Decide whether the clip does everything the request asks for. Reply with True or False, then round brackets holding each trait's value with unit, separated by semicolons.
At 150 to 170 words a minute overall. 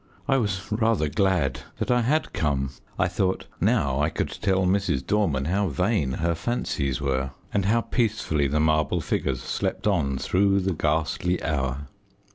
True (160 wpm)